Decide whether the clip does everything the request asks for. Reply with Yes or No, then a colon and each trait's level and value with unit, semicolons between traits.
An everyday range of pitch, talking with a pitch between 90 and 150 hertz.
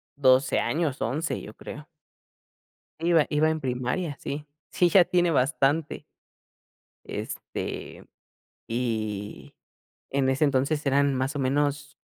Yes: average, 3.1 semitones; medium, 140 Hz